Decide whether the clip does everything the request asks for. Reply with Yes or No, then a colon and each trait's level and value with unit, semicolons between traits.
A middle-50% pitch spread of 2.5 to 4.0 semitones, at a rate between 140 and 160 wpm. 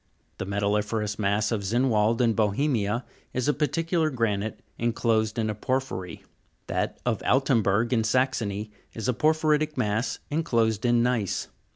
Yes: average, 3.7 semitones; average, 145 wpm